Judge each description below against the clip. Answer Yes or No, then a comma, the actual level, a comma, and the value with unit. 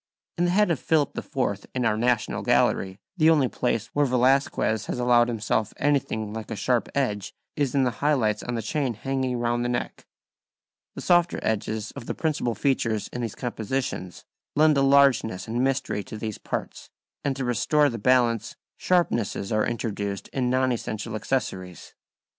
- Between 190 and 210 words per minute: No, average, 175 wpm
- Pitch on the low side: Yes, low, 120 Hz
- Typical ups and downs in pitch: Yes, average, 3.8 semitones